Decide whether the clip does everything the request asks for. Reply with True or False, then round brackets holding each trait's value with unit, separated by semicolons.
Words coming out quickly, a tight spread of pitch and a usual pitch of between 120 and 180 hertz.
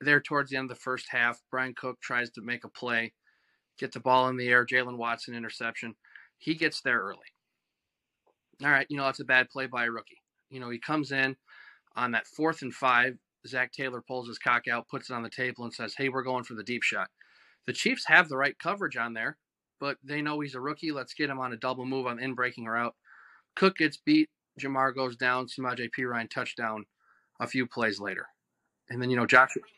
True (230 wpm; 2.0 semitones; 125 Hz)